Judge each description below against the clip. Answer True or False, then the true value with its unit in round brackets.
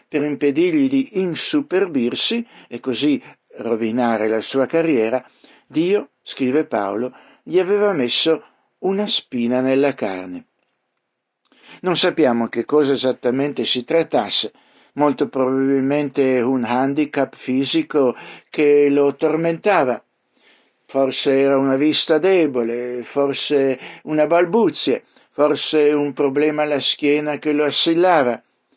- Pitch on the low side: False (145 Hz)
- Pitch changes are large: False (4.1 semitones)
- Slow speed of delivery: True (105 wpm)